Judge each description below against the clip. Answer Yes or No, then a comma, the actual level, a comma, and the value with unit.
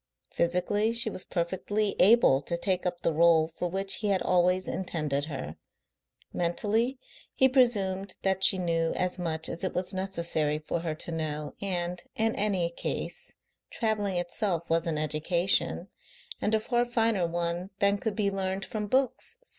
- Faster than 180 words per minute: No, average, 160 wpm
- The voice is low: No, medium, 185 Hz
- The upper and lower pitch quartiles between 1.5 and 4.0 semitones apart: Yes, average, 3.3 semitones